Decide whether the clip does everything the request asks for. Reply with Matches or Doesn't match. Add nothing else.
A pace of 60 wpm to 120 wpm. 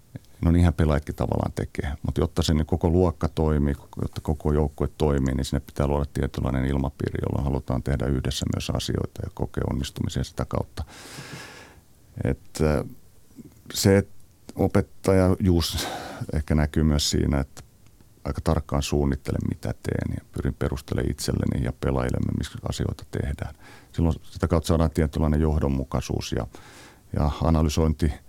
Doesn't match